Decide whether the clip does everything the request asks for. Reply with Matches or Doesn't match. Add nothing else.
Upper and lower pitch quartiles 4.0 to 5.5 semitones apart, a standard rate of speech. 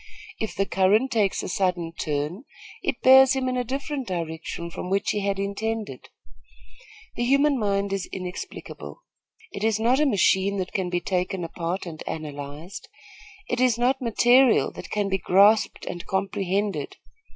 Matches